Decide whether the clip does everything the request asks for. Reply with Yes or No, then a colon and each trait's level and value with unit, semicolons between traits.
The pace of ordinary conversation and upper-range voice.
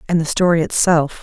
No: average, 195 wpm; medium, 165 Hz